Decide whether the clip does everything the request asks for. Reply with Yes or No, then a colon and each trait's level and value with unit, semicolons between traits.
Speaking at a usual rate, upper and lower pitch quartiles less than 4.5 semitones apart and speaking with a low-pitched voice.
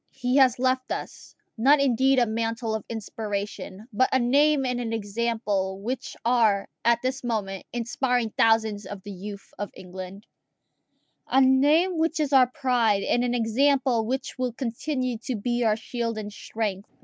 No: average, 160 wpm; average, 3.4 semitones; high, 235 Hz